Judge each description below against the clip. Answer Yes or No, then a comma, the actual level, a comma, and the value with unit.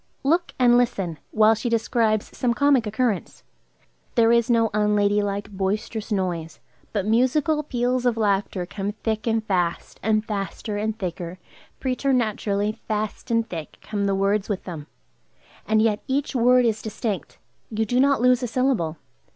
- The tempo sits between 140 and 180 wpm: Yes, average, 150 wpm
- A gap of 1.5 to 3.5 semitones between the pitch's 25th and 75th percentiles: Yes, average, 3.1 semitones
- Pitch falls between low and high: No, high, 220 Hz